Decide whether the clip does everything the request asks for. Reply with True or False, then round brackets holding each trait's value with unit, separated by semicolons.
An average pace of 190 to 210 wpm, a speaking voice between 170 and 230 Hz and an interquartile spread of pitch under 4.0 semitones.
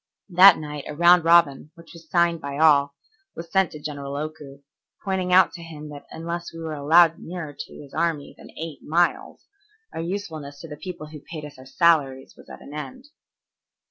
False (195 wpm; 160 Hz; 2.8 semitones)